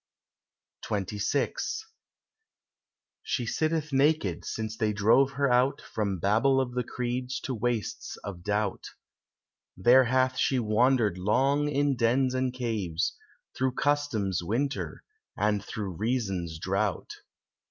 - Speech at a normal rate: No, slow, 115 wpm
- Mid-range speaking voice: No, low, 120 Hz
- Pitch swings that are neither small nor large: Yes, average, 4.3 semitones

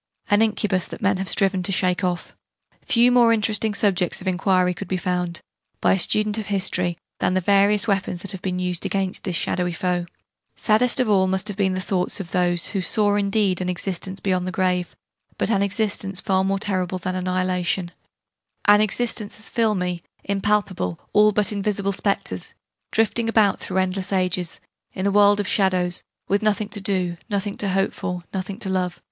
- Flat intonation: Yes, narrow, 2.1 semitones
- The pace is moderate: Yes, average, 190 wpm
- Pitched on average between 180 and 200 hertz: Yes, high, 190 Hz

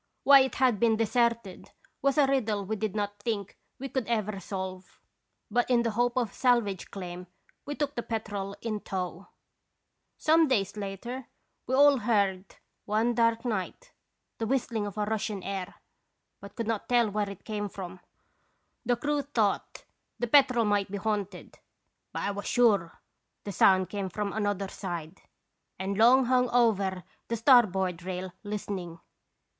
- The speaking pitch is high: Yes, high, 210 Hz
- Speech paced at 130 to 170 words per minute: Yes, average, 160 wpm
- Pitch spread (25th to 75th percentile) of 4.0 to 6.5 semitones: No, average, 3.6 semitones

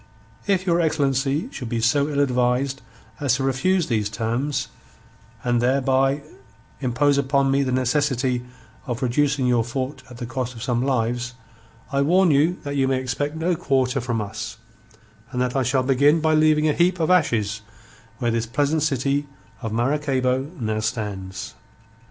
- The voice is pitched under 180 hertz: Yes, low, 135 Hz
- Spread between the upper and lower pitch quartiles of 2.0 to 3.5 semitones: Yes, average, 3.0 semitones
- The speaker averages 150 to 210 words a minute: Yes, average, 165 wpm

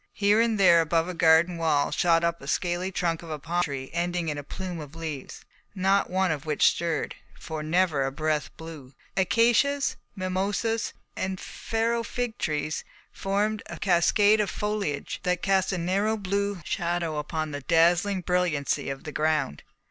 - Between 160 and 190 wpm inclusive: Yes, average, 170 wpm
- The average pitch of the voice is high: No, medium, 175 Hz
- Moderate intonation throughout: Yes, average, 3.9 semitones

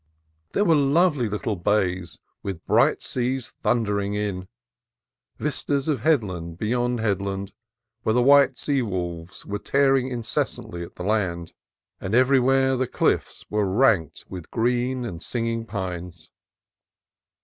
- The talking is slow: Yes, slow, 130 wpm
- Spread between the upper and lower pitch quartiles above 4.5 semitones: Yes, wide, 5.6 semitones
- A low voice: Yes, low, 110 Hz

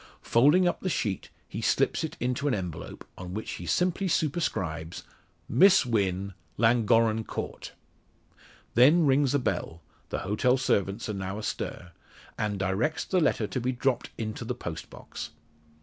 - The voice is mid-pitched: No, low, 115 Hz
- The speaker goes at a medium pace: Yes, average, 150 wpm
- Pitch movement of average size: No, wide, 6.4 semitones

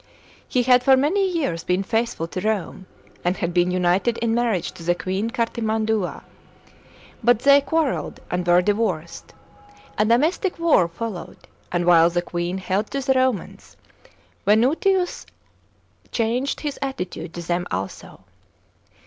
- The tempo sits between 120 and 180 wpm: Yes, average, 140 wpm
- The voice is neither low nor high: No, high, 215 Hz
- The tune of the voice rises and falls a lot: Yes, wide, 6.5 semitones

